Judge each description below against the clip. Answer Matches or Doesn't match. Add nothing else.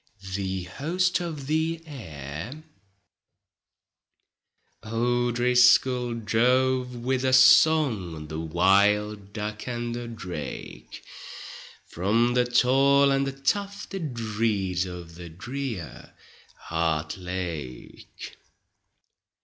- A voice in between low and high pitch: Doesn't match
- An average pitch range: Doesn't match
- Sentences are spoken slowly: Matches